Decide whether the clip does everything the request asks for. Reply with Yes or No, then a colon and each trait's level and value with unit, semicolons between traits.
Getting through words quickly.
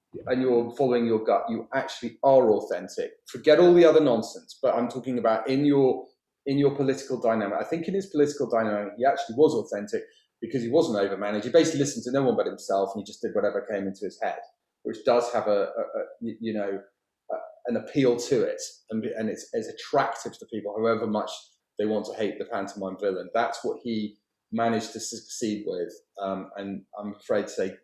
Yes: fast, 210 wpm